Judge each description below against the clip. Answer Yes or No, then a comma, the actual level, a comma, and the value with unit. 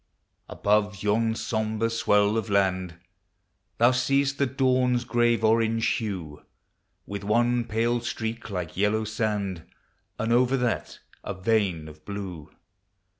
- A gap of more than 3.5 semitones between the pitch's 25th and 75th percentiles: No, average, 2.9 semitones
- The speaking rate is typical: No, slow, 125 wpm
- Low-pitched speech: Yes, low, 110 Hz